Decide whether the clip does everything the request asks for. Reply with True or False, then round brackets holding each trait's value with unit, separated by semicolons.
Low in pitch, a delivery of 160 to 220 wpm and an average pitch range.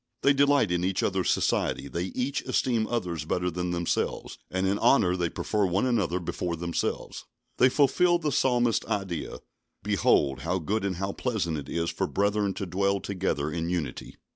True (95 Hz; 175 wpm; 4.3 semitones)